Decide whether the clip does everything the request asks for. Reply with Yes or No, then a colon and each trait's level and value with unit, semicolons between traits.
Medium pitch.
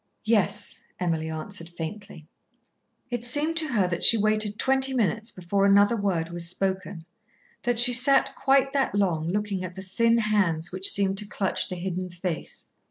No: high, 200 Hz